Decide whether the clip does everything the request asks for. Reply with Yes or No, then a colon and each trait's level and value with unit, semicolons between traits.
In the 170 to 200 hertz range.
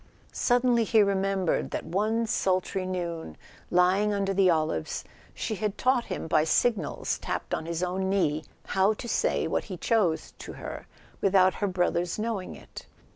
Yes: high, 190 Hz